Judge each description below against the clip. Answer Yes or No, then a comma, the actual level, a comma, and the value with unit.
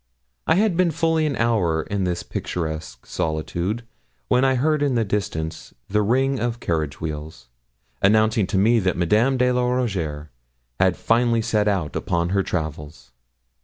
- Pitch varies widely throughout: Yes, wide, 7.2 semitones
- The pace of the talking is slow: No, average, 160 wpm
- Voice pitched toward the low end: Yes, low, 105 Hz